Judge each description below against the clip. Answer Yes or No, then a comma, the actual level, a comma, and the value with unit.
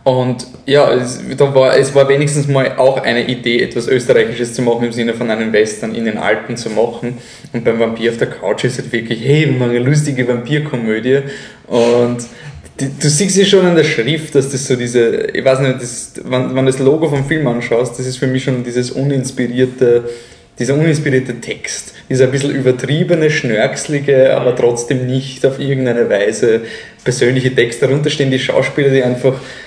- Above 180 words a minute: Yes, fast, 190 wpm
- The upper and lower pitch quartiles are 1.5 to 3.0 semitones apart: Yes, narrow, 2.4 semitones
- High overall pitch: No, low, 130 Hz